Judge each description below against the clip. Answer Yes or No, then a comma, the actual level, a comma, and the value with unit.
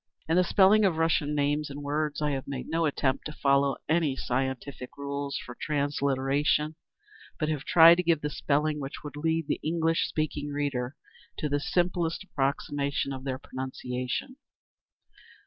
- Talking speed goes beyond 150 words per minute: Yes, average, 160 wpm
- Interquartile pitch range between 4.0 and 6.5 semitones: No, narrow, 2.4 semitones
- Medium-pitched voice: Yes, medium, 145 Hz